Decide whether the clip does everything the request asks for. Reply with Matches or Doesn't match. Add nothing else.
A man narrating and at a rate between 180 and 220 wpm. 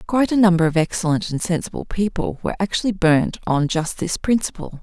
Doesn't match